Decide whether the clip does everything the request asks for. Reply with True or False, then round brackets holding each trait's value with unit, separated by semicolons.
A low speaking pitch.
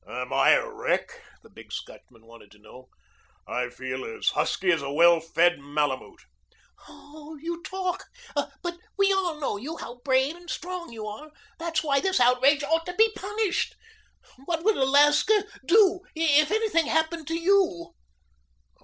False (300 Hz)